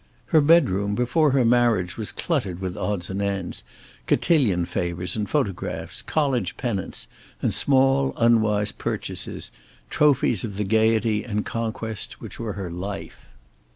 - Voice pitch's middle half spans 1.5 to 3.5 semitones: No, average, 4.2 semitones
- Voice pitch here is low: Yes, low, 110 Hz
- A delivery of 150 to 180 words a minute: No, slow, 135 wpm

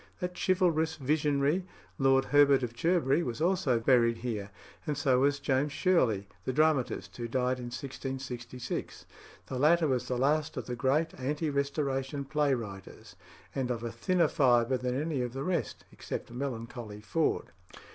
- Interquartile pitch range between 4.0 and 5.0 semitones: No, average, 3.4 semitones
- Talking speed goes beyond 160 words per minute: No, average, 155 wpm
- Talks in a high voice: No, low, 135 Hz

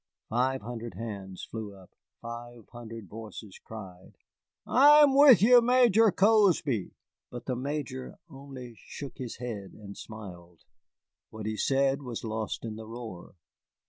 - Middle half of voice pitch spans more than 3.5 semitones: Yes, average, 4.5 semitones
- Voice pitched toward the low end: Yes, low, 120 Hz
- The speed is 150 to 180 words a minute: No, slow, 135 wpm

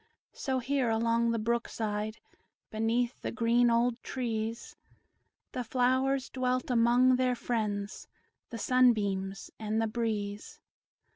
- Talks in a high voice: Yes, high, 235 Hz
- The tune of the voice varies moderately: No, narrow, 2.3 semitones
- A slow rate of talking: Yes, slow, 120 wpm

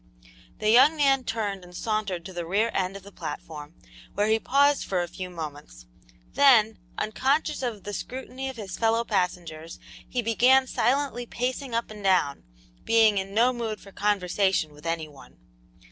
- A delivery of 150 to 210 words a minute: Yes, average, 170 wpm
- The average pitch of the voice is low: No, high, 210 Hz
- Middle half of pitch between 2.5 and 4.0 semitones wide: No, average, 5.2 semitones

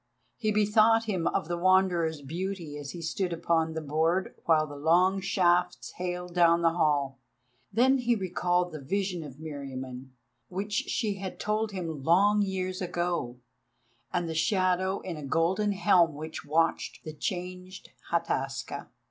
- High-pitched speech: No, medium, 175 Hz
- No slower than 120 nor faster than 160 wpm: Yes, average, 150 wpm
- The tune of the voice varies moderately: Yes, average, 3.1 semitones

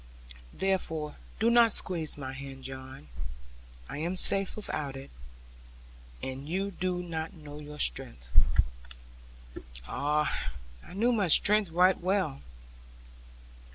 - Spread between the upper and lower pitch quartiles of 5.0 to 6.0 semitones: Yes, wide, 5.6 semitones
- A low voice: No, medium, 160 Hz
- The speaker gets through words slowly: Yes, slow, 115 wpm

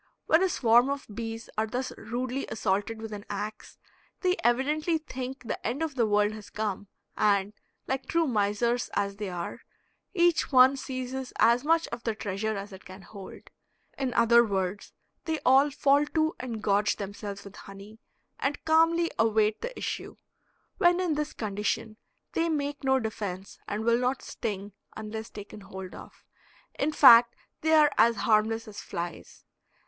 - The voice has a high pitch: Yes, high, 230 Hz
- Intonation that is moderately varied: Yes, average, 4.9 semitones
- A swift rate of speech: No, average, 165 wpm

